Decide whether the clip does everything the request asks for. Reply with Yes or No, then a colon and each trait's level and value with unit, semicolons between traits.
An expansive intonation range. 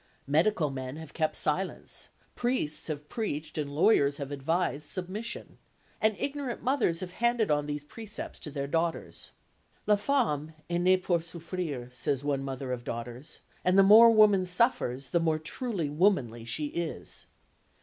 Yes: wide, 5.7 semitones